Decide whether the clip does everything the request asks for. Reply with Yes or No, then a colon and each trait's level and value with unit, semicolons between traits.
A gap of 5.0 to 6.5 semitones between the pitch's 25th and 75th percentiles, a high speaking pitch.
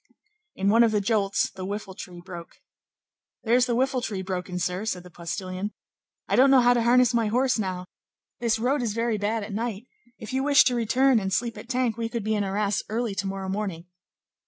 No: average, 3.8 semitones; high, 215 Hz